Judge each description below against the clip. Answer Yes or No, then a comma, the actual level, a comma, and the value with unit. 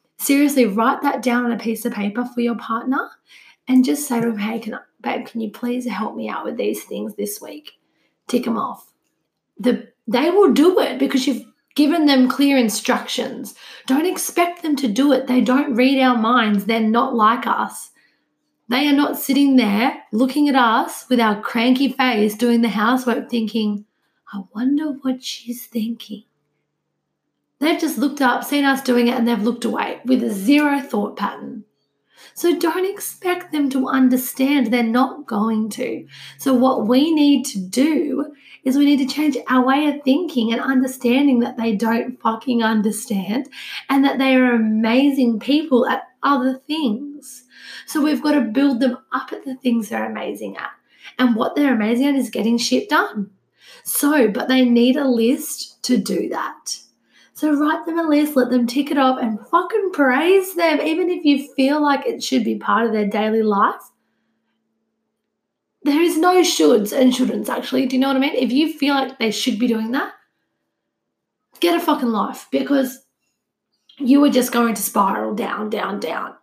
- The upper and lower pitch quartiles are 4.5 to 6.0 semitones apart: No, average, 3.5 semitones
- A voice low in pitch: No, very high, 255 Hz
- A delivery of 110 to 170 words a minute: No, average, 185 wpm